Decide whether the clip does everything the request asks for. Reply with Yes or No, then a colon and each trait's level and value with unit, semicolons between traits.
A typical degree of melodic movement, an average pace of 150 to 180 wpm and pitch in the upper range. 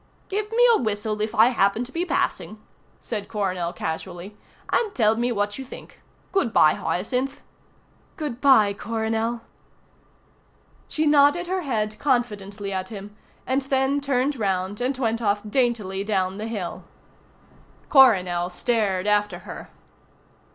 No: average, 4.7 semitones; slow, 135 wpm; high, 220 Hz